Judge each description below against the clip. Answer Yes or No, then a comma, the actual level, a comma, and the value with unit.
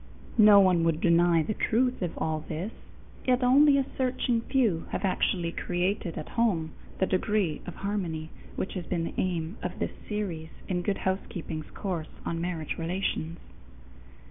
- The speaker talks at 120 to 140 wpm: No, average, 160 wpm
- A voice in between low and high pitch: Yes, medium, 180 Hz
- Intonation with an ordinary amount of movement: Yes, average, 4.1 semitones